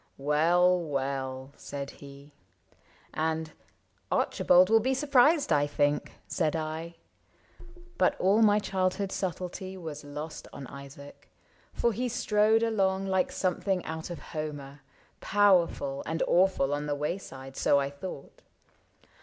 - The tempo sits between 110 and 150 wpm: Yes, average, 140 wpm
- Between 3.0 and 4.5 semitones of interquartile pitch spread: No, average, 5.0 semitones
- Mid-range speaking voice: Yes, medium, 160 Hz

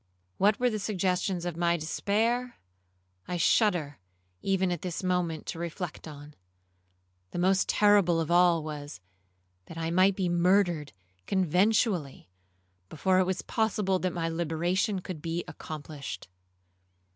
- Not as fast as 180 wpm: Yes, slow, 135 wpm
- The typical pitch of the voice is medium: Yes, medium, 180 Hz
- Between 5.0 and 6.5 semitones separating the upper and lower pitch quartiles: No, average, 2.9 semitones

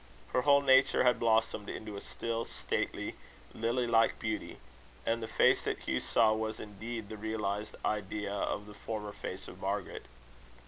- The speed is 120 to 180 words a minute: Yes, average, 165 wpm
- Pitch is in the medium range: No, low, 110 Hz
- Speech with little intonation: Yes, narrow, 1.8 semitones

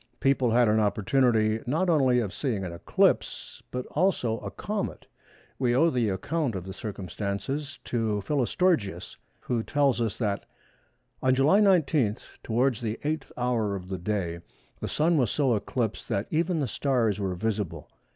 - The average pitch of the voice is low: Yes, low, 120 Hz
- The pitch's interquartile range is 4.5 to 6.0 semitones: Yes, wide, 5.4 semitones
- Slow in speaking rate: No, average, 155 wpm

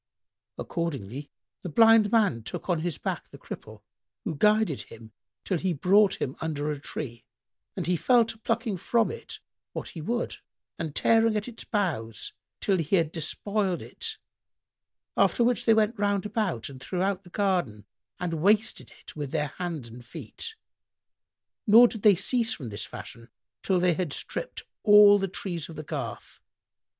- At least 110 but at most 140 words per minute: No, average, 165 wpm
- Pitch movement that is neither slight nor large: No, wide, 6.1 semitones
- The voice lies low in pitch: No, medium, 185 Hz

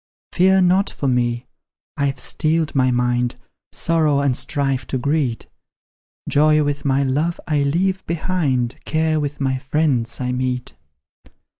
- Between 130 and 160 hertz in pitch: Yes, medium, 140 Hz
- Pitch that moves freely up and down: No, average, 3.7 semitones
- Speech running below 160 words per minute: Yes, slow, 135 wpm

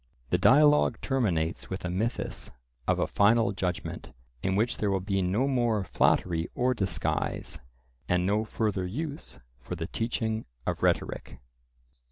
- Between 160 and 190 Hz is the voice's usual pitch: No, low, 105 Hz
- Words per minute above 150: No, average, 145 wpm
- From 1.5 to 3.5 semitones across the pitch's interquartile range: No, average, 4.5 semitones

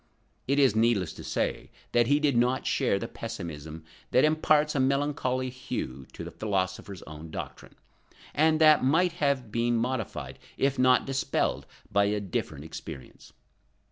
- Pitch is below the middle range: Yes, low, 120 Hz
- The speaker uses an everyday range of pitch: No, wide, 6.3 semitones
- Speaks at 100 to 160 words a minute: Yes, average, 150 wpm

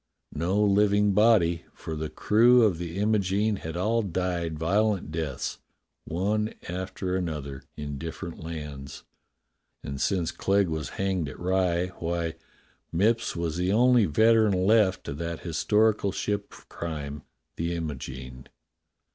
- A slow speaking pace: Yes, slow, 130 wpm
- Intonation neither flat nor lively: Yes, average, 4.4 semitones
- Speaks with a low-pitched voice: Yes, very low, 90 Hz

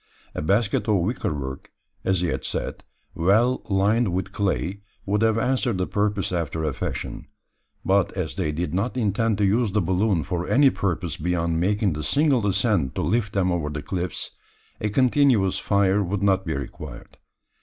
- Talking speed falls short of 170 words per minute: No, average, 175 wpm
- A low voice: Yes, very low, 95 Hz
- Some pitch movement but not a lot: Yes, average, 3.7 semitones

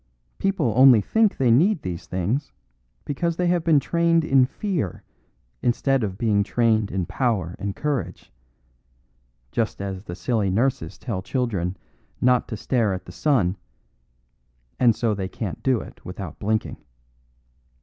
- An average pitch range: No, wide, 5.7 semitones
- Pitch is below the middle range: Yes, low, 115 Hz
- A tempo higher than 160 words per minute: No, average, 145 wpm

